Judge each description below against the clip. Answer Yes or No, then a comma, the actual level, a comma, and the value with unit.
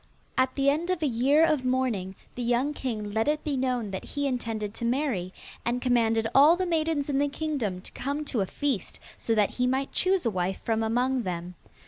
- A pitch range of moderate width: Yes, average, 4.5 semitones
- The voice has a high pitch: Yes, very high, 255 Hz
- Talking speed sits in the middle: No, fast, 215 wpm